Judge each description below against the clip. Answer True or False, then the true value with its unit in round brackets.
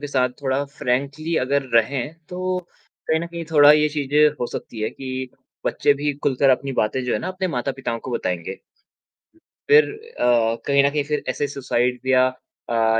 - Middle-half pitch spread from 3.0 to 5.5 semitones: True (3.3 semitones)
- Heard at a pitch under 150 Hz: True (140 Hz)